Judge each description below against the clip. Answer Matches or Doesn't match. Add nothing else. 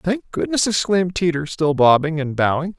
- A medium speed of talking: Matches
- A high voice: Doesn't match